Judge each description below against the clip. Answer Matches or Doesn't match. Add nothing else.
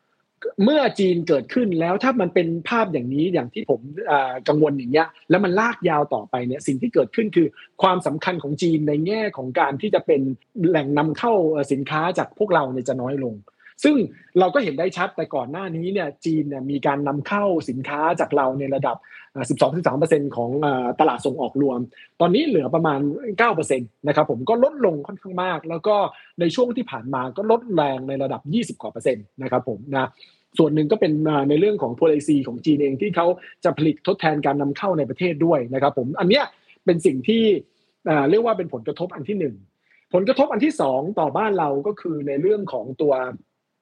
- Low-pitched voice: Doesn't match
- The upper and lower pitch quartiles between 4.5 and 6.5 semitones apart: Matches